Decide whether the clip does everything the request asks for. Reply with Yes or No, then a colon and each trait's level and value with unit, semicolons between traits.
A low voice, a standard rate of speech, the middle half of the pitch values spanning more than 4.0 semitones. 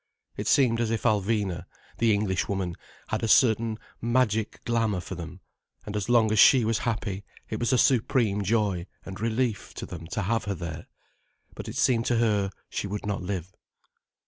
No: low, 105 Hz; average, 180 wpm; average, 3.1 semitones